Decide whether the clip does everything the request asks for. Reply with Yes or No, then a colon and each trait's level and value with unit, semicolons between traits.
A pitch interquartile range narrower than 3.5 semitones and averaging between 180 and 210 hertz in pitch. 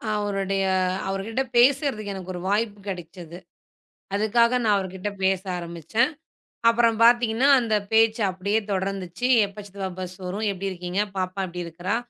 Yes: average, 3.1 semitones; high, 200 Hz